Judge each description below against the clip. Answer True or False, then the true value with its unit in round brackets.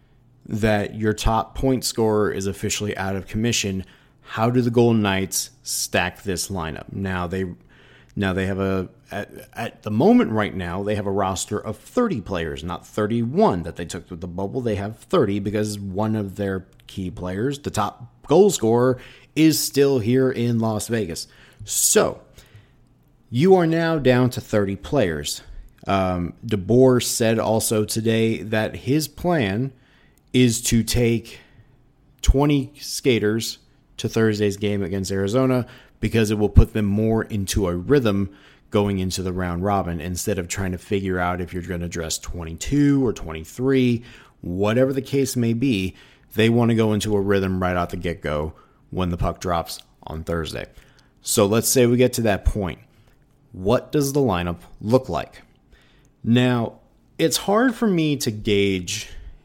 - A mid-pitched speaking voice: False (110 Hz)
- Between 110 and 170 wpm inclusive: True (165 wpm)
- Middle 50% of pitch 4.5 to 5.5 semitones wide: True (4.8 semitones)